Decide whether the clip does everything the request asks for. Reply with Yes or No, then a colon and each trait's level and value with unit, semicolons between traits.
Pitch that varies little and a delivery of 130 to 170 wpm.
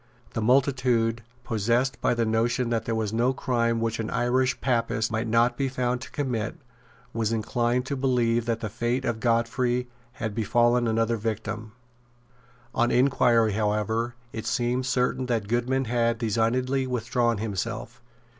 Yes: narrow, 1.8 semitones; average, 150 wpm